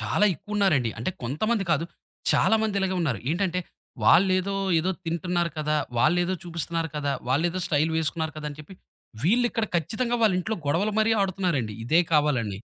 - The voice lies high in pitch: No, medium, 170 Hz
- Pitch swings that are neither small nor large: Yes, average, 4.6 semitones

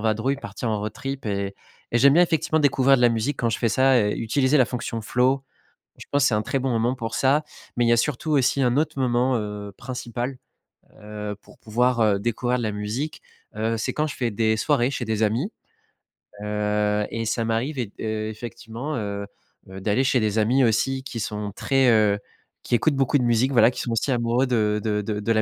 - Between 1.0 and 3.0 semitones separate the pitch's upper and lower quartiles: No, average, 3.5 semitones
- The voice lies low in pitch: Yes, low, 120 Hz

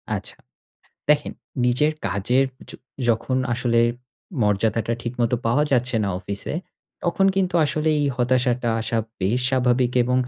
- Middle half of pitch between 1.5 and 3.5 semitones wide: Yes, narrow, 2.4 semitones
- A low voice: Yes, low, 125 Hz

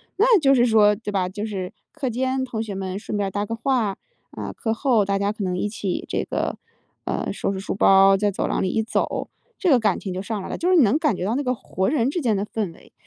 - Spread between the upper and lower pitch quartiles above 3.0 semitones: Yes, average, 4.4 semitones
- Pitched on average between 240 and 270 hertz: No, high, 215 Hz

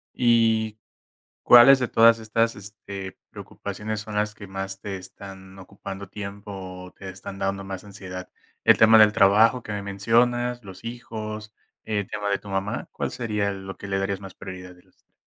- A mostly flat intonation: Yes, narrow, 2.2 semitones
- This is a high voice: No, low, 100 Hz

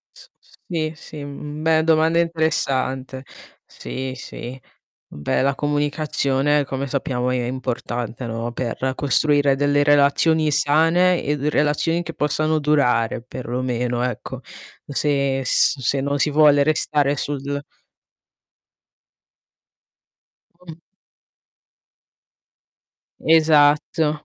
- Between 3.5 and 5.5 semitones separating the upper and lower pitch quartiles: No, average, 2.7 semitones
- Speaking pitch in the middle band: Yes, medium, 145 Hz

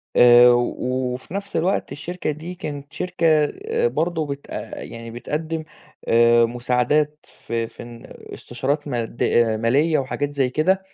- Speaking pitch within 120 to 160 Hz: Yes, medium, 140 Hz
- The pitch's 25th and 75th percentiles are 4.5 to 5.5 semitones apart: Yes, average, 5.0 semitones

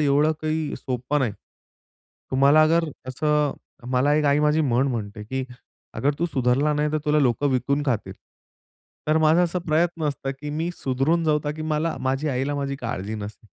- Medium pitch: Yes, medium, 145 Hz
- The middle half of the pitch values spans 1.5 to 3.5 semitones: Yes, average, 3.0 semitones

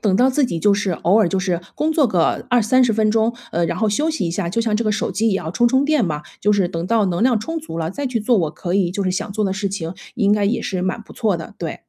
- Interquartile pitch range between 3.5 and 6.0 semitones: Yes, average, 4.1 semitones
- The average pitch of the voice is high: Yes, high, 205 Hz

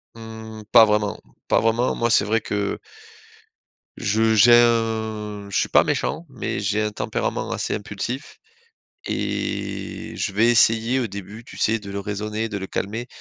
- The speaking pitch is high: No, low, 110 Hz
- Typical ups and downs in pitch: No, narrow, 1.7 semitones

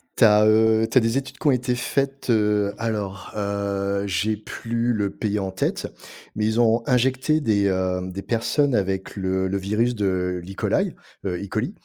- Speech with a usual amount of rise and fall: Yes, average, 3.1 semitones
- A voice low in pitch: Yes, low, 105 Hz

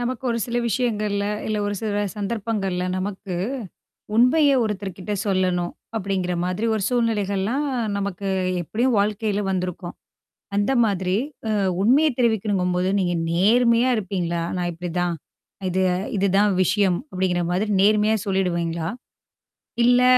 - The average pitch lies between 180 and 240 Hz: Yes, high, 200 Hz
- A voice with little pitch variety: No, average, 3.3 semitones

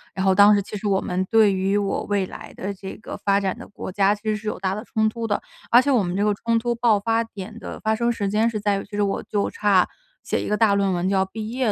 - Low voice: No, high, 205 Hz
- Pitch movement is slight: Yes, narrow, 2.2 semitones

